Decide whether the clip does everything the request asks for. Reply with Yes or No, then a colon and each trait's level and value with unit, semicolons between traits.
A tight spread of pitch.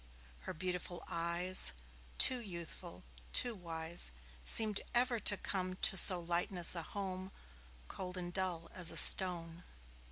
Yes: narrow, 1.9 semitones